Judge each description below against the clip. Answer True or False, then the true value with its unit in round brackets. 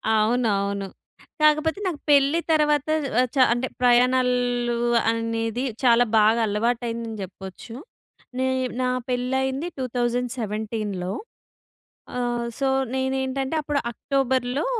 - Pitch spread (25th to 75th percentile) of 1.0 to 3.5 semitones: True (2.6 semitones)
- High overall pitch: True (245 Hz)